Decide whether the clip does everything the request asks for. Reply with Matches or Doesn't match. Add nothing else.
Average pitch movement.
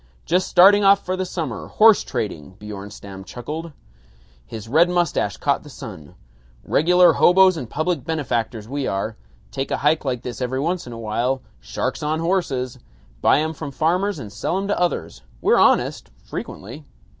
Doesn't match